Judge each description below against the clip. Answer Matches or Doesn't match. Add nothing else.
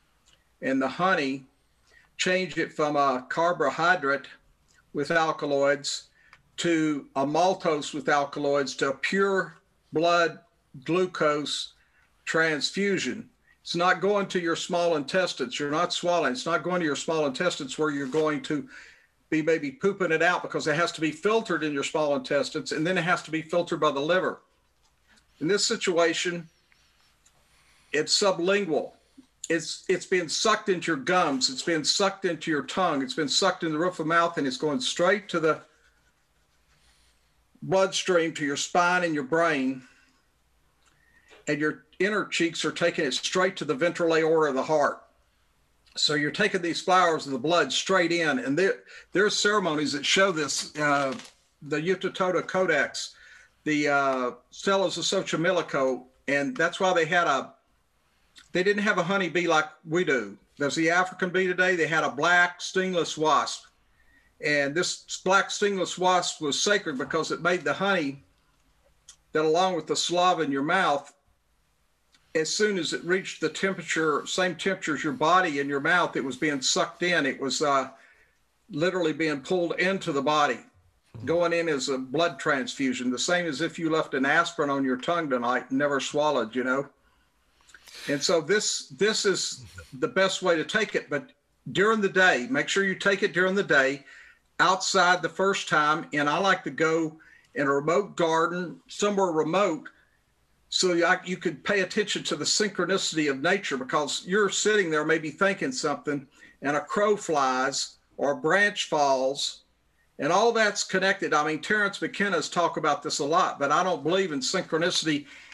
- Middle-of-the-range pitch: Matches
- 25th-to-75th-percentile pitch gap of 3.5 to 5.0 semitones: Matches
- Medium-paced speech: Matches